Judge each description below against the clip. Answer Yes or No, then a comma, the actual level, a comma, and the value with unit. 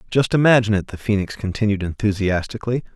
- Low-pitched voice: Yes, low, 105 Hz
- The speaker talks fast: No, average, 140 wpm